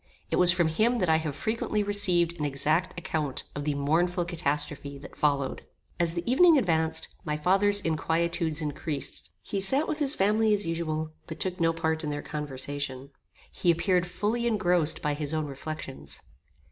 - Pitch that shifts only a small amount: No, average, 3.9 semitones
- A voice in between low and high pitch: Yes, medium, 165 Hz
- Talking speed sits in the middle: Yes, average, 170 wpm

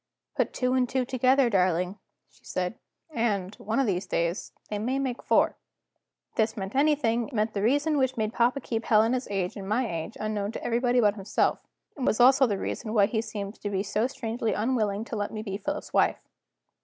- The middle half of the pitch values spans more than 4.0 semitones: No, average, 3.7 semitones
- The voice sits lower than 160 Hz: No, high, 225 Hz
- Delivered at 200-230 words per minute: Yes, fast, 205 wpm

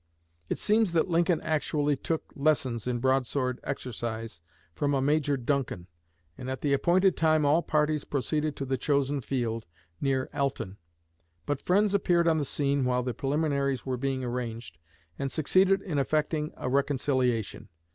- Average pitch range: Yes, average, 3.4 semitones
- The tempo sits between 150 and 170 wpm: Yes, average, 155 wpm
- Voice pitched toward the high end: No, medium, 140 Hz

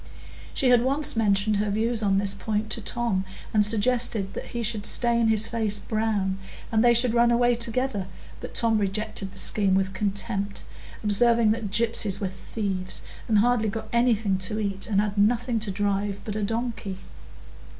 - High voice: Yes, high, 215 Hz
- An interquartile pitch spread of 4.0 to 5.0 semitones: No, average, 2.7 semitones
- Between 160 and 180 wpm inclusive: Yes, average, 175 wpm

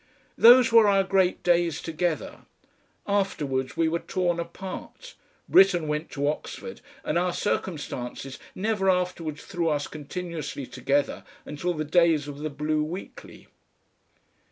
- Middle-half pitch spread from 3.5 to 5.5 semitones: Yes, average, 3.8 semitones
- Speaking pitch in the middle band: Yes, medium, 170 Hz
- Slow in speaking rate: Yes, slow, 130 wpm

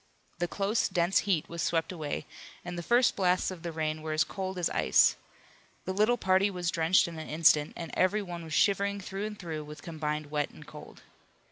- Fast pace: Yes, fast, 210 wpm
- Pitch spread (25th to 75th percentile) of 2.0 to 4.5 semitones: Yes, average, 3.4 semitones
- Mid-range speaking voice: Yes, medium, 175 Hz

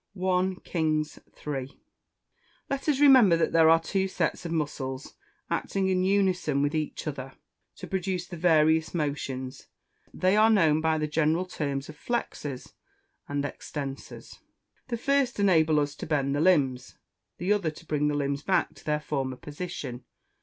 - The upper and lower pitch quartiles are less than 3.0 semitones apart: No, average, 4.3 semitones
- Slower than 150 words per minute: No, average, 160 wpm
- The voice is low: No, medium, 160 Hz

